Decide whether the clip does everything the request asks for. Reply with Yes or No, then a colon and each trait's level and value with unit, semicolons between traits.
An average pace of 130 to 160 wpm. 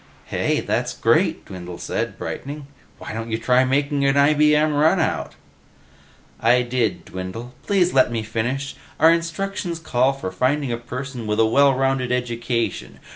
Yes: average, 150 wpm